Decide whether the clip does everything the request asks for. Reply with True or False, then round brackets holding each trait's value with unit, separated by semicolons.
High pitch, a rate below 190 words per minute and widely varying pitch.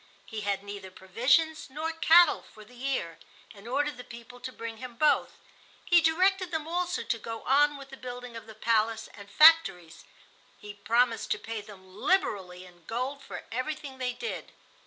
True (245 Hz; 180 wpm; 5.8 semitones)